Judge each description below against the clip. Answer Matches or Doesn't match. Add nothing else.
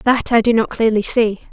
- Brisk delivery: Matches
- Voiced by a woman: Matches